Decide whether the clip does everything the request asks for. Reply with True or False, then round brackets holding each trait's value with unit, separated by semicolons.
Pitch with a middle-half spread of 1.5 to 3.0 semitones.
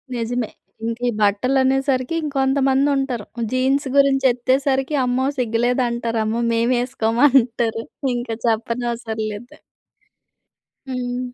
True (2.4 semitones)